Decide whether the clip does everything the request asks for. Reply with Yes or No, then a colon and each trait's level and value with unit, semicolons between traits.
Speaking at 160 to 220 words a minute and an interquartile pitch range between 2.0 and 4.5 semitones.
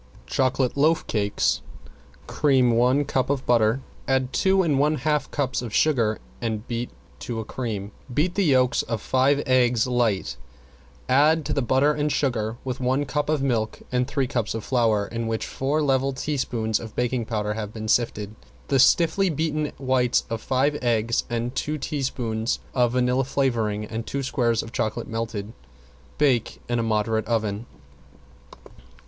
Yes: average, 165 wpm; average, 3.6 semitones